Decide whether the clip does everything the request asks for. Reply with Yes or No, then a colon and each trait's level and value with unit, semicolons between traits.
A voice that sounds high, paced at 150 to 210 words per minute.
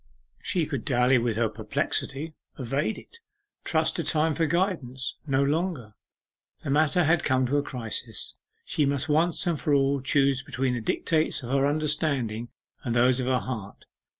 No: medium, 140 Hz; average, 170 wpm